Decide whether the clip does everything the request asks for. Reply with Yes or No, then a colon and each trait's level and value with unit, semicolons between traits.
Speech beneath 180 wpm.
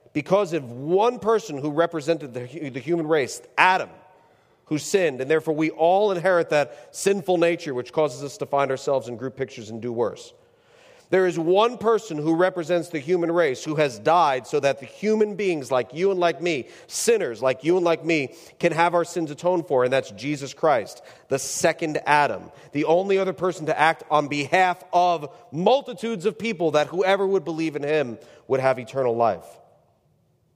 No: average, 190 wpm